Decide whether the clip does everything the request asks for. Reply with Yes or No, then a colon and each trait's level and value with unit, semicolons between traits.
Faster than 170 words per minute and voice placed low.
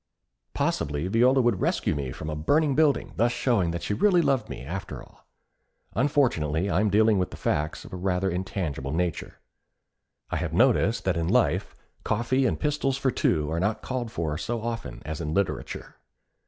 Yes: average, 180 wpm; very low, 95 Hz